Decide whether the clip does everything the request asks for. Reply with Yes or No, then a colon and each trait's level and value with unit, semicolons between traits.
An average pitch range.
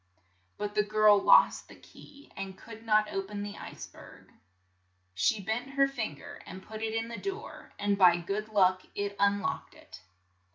No: narrow, 2.3 semitones